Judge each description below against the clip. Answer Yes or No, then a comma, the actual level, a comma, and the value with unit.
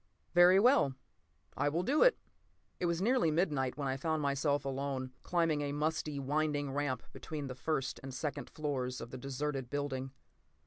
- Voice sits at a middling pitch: Yes, medium, 145 Hz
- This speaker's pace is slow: No, average, 170 wpm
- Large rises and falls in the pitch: No, average, 3.0 semitones